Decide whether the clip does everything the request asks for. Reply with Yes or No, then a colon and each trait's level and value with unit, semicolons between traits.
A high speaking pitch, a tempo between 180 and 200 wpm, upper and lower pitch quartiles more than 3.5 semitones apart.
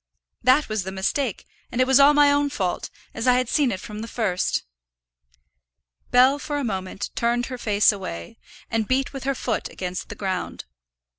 Yes: high, 235 Hz; average, 190 wpm; average, 5.3 semitones